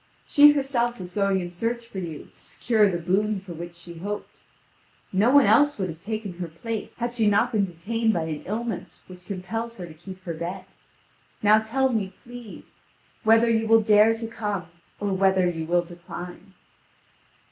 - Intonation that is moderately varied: Yes, average, 4.3 semitones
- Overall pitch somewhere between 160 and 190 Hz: No, high, 205 Hz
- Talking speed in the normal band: Yes, average, 185 wpm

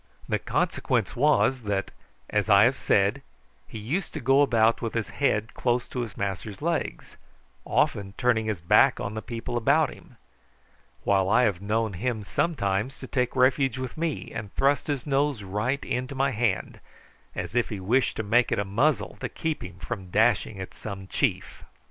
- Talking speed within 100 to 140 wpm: No, average, 180 wpm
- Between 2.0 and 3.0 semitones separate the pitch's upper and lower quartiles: No, average, 4.7 semitones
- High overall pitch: No, low, 115 Hz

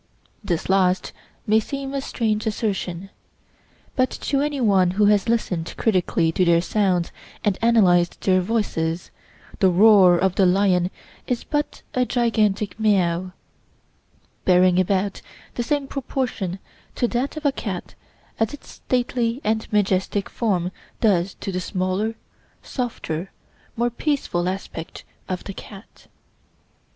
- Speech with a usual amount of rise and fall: Yes, average, 4.2 semitones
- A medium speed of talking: No, slow, 130 wpm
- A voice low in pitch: No, high, 200 Hz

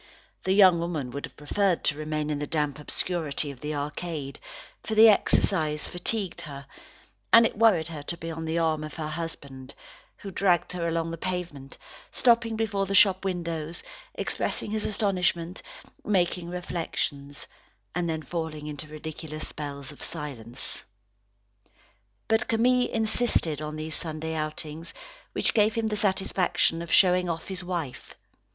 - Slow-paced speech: No, average, 155 wpm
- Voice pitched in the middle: Yes, medium, 165 Hz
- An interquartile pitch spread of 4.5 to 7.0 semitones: No, average, 3.7 semitones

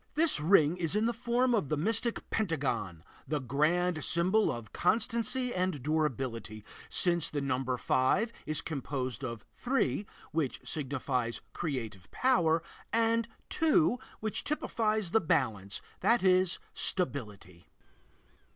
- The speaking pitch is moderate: Yes, medium, 160 Hz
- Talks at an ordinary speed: No, slow, 125 wpm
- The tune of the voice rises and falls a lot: Yes, wide, 9.0 semitones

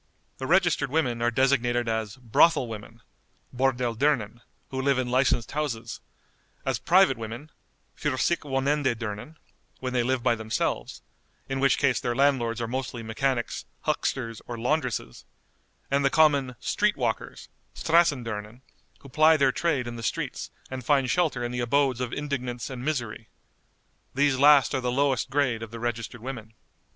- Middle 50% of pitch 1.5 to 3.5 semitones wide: Yes, average, 3.1 semitones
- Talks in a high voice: No, low, 130 Hz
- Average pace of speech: Yes, average, 160 wpm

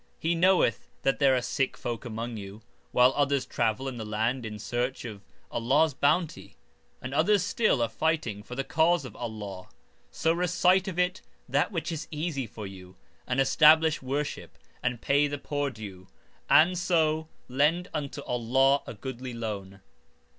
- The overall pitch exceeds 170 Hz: No, low, 135 Hz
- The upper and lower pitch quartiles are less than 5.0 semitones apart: No, wide, 5.4 semitones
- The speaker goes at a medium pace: Yes, average, 165 wpm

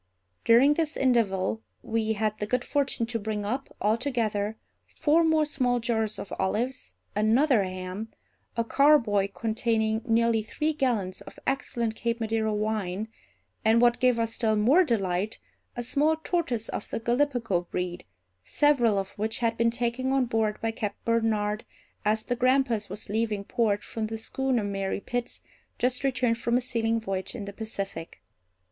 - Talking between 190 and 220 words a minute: No, average, 160 wpm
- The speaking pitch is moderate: No, high, 225 Hz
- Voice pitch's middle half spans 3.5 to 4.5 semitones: No, average, 2.8 semitones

